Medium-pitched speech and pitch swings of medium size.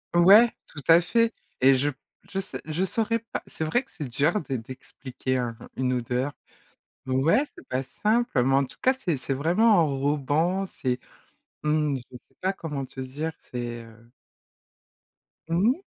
No: medium, 145 Hz; wide, 6.4 semitones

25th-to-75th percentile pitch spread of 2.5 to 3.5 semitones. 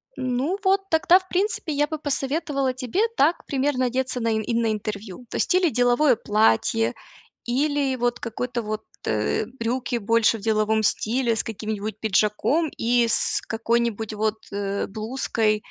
No: average, 4.1 semitones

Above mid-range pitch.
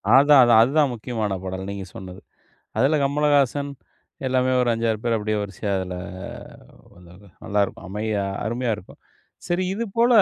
No: low, 115 Hz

